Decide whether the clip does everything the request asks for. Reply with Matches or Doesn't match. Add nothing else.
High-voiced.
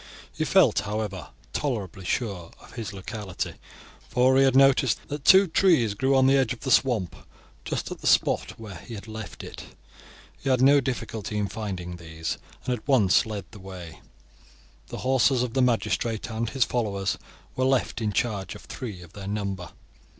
Doesn't match